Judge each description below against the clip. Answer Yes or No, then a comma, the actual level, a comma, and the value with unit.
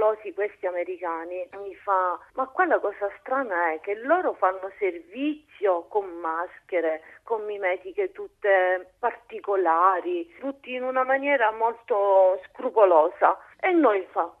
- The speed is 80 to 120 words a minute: Yes, slow, 115 wpm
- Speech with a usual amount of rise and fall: No, wide, 5.9 semitones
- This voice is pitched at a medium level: No, high, 200 Hz